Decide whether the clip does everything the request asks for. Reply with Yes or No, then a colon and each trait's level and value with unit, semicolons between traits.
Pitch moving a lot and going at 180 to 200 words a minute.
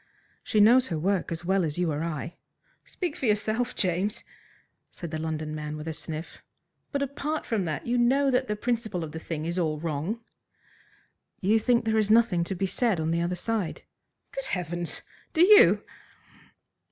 Yes: wide, 6.4 semitones; average, 185 wpm